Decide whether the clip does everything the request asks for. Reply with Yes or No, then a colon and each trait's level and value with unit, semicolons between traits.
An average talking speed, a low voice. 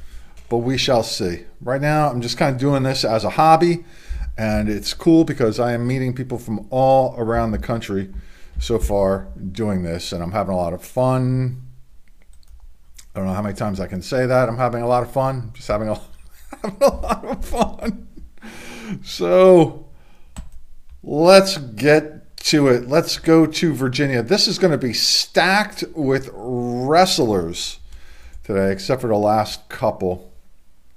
Yes: average, 170 wpm; low, 120 Hz